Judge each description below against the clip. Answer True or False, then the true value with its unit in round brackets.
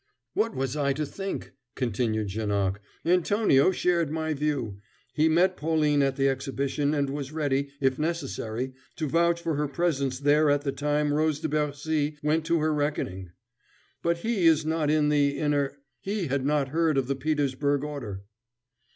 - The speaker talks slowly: False (170 wpm)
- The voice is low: False (145 Hz)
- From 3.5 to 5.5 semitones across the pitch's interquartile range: False (2.7 semitones)